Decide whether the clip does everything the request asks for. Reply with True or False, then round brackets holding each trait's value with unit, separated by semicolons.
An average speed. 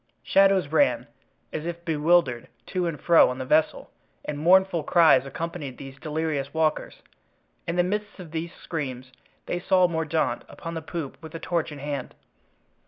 True (165 wpm)